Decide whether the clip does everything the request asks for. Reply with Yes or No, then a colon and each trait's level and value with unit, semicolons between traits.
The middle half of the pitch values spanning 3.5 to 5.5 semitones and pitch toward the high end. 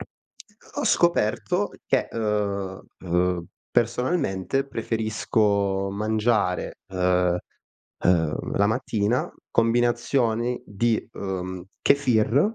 No: average, 3.9 semitones; low, 110 Hz